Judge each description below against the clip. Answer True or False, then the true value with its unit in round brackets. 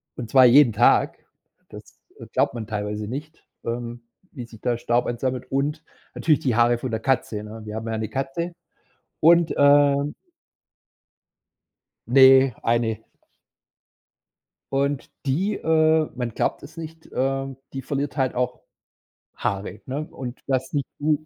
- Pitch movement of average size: True (3.5 semitones)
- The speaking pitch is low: True (130 Hz)